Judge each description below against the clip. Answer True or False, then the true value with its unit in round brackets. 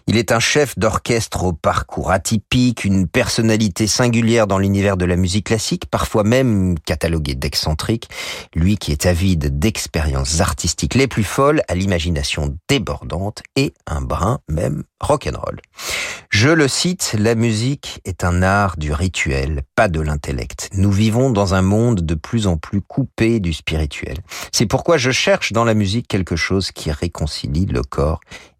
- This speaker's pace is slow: False (160 wpm)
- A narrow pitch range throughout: False (5.2 semitones)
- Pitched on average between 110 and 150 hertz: False (95 Hz)